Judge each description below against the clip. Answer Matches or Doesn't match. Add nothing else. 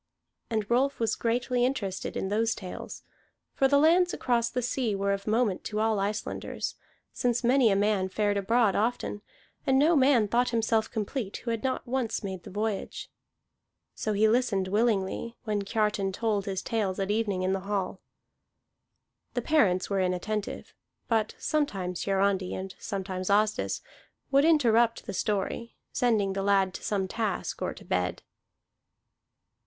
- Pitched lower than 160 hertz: Doesn't match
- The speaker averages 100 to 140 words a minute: Doesn't match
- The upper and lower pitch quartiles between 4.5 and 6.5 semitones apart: Doesn't match